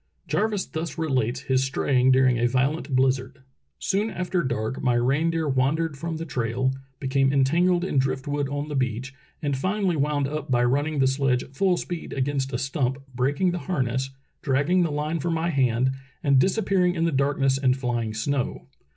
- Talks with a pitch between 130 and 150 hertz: Yes, medium, 140 Hz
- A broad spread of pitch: No, average, 3.8 semitones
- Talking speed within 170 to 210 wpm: Yes, average, 180 wpm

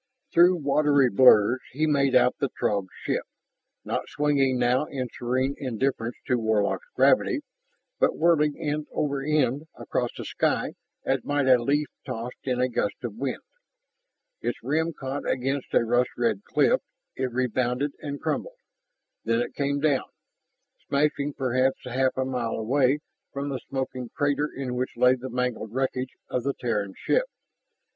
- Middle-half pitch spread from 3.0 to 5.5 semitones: No, narrow, 2.6 semitones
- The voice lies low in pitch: Yes, low, 130 Hz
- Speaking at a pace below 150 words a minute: No, average, 155 wpm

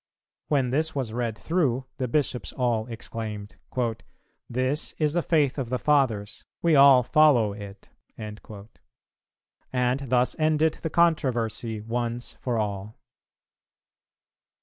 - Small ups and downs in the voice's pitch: No, average, 4.6 semitones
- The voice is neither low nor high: No, low, 125 Hz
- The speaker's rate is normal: No, slow, 115 wpm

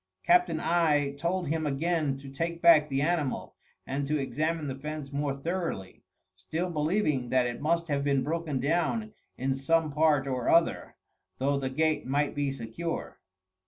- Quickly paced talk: No, average, 160 wpm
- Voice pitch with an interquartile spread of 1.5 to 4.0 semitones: Yes, average, 3.4 semitones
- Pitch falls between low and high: Yes, medium, 150 Hz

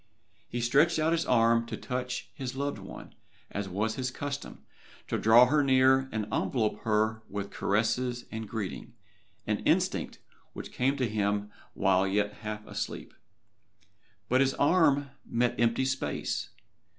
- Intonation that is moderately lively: Yes, average, 3.8 semitones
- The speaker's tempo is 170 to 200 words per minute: No, average, 145 wpm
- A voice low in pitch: Yes, low, 120 Hz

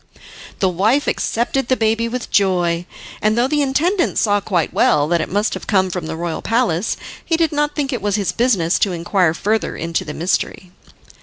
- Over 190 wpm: Yes, average, 200 wpm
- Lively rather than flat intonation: Yes, wide, 6.3 semitones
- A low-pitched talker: No, high, 205 Hz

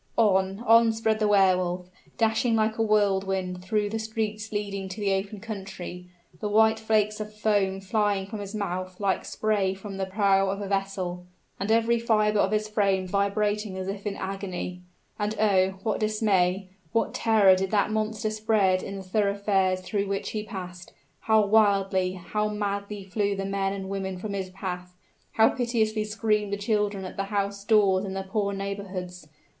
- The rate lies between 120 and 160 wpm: No, average, 180 wpm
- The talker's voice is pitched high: Yes, high, 200 Hz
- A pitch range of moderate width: No, narrow, 1.9 semitones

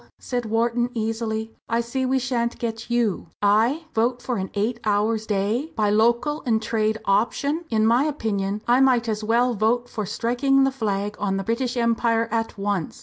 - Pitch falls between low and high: No, high, 230 Hz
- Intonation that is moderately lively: No, narrow, 2.3 semitones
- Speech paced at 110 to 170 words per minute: No, average, 180 wpm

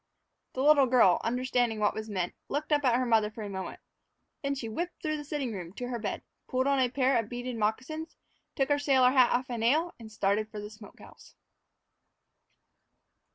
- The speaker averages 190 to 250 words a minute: Yes, average, 200 wpm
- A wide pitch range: No, average, 4.2 semitones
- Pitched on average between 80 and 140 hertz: No, high, 245 Hz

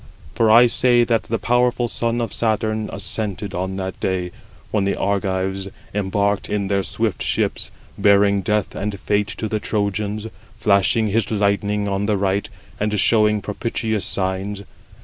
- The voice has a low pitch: Yes, low, 105 Hz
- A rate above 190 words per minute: No, average, 155 wpm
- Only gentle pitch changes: Yes, narrow, 1.8 semitones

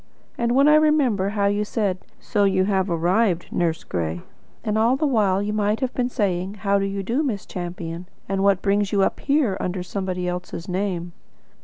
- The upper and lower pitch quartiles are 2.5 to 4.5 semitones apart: Yes, average, 3.2 semitones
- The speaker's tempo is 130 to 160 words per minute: No, average, 195 wpm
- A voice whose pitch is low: No, high, 200 Hz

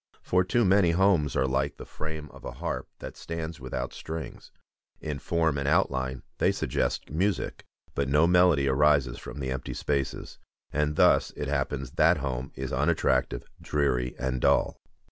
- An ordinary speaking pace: Yes, average, 165 wpm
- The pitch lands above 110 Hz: No, very low, 75 Hz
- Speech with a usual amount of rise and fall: Yes, average, 3.7 semitones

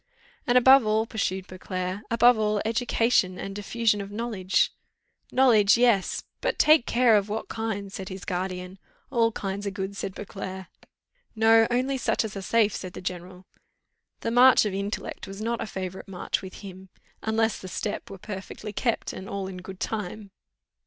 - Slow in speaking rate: No, average, 180 wpm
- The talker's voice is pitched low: No, high, 205 Hz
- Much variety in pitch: No, average, 3.1 semitones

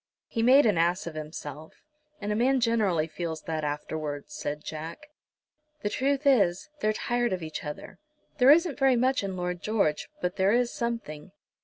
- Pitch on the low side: No, high, 195 Hz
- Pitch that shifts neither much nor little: No, wide, 7.3 semitones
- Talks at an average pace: Yes, average, 175 wpm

